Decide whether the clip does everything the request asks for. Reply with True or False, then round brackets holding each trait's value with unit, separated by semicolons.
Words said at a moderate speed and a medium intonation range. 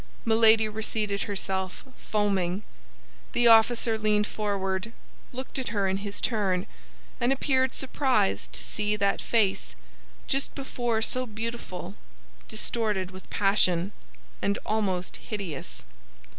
False (115 wpm; 3.2 semitones)